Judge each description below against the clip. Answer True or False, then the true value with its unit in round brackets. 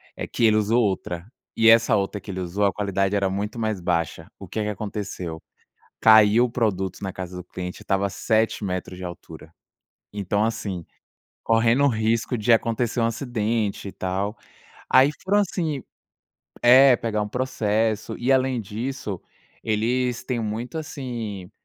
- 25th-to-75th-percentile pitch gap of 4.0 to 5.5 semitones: False (3.4 semitones)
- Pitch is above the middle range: False (110 Hz)